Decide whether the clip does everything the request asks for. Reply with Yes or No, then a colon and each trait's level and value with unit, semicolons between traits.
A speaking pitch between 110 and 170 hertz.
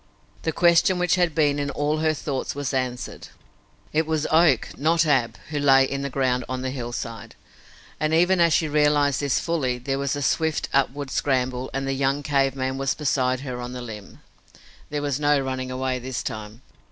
Yes: medium, 140 Hz